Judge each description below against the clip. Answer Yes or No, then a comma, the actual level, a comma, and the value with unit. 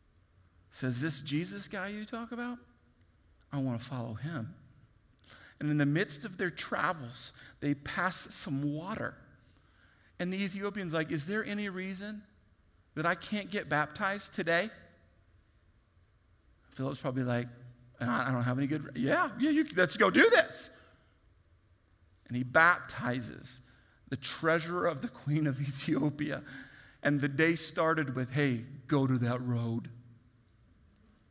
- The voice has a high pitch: No, low, 135 Hz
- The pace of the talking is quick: No, average, 140 wpm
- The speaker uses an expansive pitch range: Yes, wide, 6.8 semitones